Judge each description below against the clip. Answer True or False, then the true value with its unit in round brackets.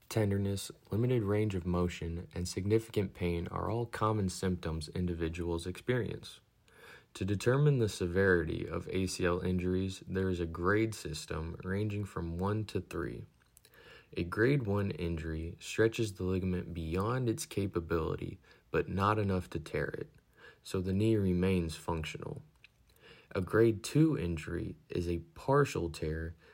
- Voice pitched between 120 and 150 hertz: False (95 Hz)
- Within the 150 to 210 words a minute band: False (135 wpm)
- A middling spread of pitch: True (3.7 semitones)